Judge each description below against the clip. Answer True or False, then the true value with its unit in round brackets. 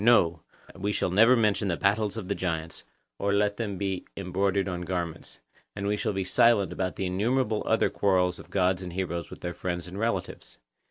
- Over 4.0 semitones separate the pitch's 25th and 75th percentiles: False (2.4 semitones)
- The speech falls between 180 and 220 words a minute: True (200 wpm)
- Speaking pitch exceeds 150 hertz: False (95 Hz)